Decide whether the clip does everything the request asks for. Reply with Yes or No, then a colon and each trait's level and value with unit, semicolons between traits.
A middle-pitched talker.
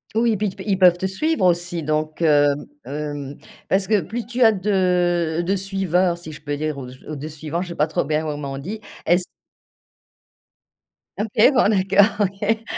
Yes: medium, 175 Hz